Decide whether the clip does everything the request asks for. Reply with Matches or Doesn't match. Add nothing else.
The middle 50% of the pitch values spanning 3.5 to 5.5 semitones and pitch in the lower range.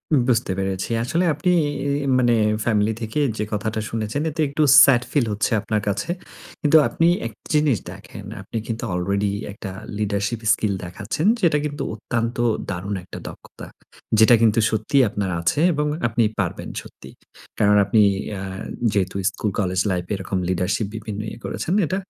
Matches